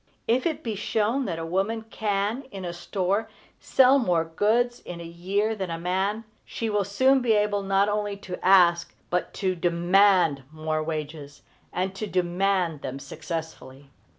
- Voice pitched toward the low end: No, high, 195 Hz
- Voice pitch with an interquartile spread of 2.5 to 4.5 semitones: Yes, average, 3.7 semitones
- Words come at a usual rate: Yes, average, 165 wpm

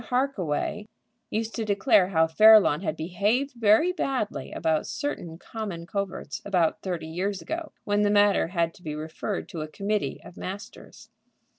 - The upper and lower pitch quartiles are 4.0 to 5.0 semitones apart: Yes, average, 4.5 semitones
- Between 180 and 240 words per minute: No, average, 155 wpm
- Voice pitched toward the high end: Yes, high, 200 Hz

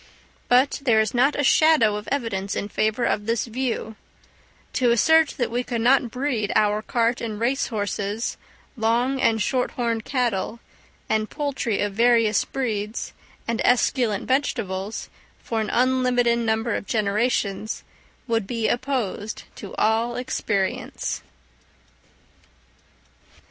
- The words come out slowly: Yes, slow, 130 wpm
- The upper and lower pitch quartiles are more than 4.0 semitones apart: No, average, 2.8 semitones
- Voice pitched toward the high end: Yes, high, 230 Hz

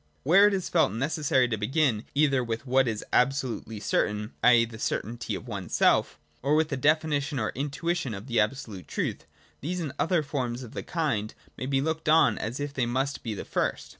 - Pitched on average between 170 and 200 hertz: No, low, 135 Hz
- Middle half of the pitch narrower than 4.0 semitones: No, average, 4.7 semitones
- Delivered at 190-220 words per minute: Yes, average, 195 wpm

